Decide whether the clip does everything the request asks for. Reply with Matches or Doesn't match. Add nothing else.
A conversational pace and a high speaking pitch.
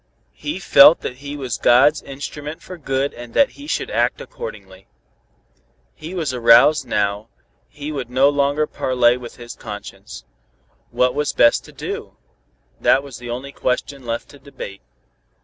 Doesn't match